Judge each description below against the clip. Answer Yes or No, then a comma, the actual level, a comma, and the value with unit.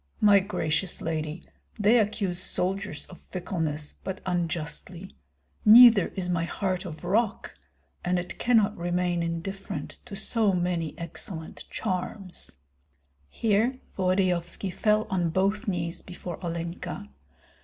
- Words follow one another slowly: Yes, slow, 115 wpm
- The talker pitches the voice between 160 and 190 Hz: Yes, medium, 185 Hz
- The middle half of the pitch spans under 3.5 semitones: Yes, average, 2.8 semitones